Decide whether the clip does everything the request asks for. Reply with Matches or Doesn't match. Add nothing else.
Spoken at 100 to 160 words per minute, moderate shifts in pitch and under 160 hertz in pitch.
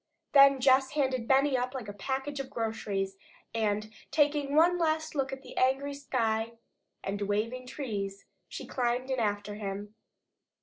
Doesn't match